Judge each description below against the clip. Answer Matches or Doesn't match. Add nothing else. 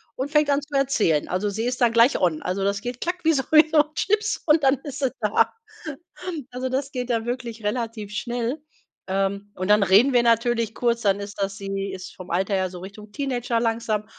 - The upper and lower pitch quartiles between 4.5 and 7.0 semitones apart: Matches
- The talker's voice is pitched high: Matches